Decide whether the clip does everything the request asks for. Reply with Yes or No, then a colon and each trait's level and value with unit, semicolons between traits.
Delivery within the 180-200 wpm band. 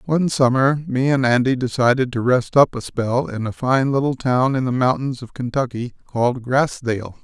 Yes: average, 190 wpm